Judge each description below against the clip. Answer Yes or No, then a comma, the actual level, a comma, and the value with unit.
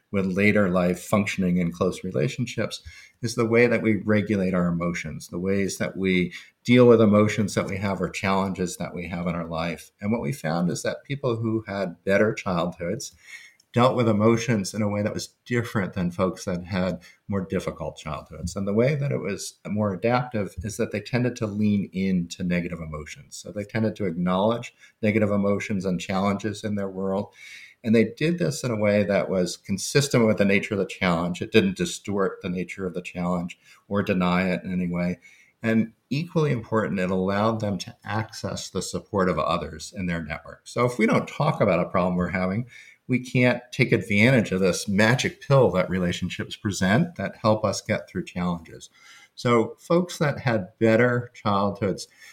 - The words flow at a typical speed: Yes, average, 190 wpm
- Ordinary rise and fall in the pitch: Yes, average, 3.7 semitones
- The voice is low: Yes, low, 100 Hz